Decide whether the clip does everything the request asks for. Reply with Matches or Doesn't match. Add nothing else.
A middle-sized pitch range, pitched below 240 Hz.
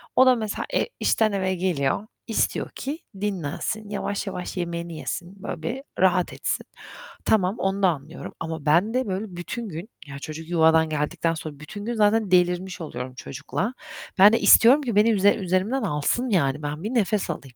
Matches